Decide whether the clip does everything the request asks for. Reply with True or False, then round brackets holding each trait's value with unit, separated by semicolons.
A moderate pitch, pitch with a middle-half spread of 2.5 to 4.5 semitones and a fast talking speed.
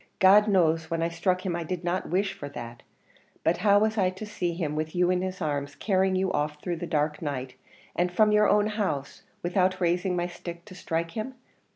True (180 Hz; 2.8 semitones; 220 wpm)